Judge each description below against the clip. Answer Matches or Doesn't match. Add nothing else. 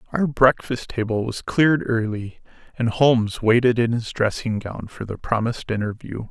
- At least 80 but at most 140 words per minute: Doesn't match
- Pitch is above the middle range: Doesn't match